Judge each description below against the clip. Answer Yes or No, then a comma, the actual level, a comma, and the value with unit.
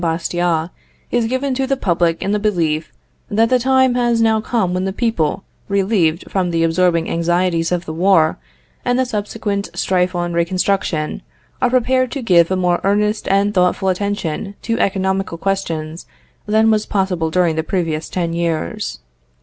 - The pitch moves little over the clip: No, average, 4.2 semitones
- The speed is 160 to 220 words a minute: Yes, average, 165 wpm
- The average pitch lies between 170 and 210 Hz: Yes, high, 190 Hz